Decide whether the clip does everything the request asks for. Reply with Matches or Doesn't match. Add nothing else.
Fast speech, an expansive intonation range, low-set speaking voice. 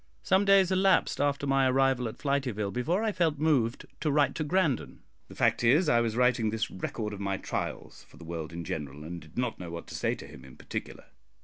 Matches